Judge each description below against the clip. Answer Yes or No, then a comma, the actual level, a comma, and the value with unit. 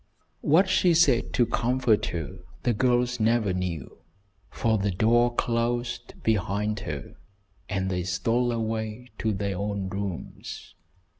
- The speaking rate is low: Yes, slow, 130 wpm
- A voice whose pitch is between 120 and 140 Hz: No, low, 110 Hz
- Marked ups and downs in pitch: No, average, 3.8 semitones